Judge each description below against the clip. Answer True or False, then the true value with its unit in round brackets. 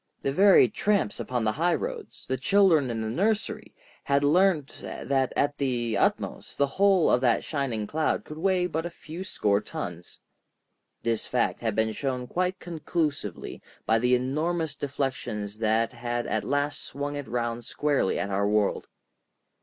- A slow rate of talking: False (160 wpm)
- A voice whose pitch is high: False (135 Hz)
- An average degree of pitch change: False (5.9 semitones)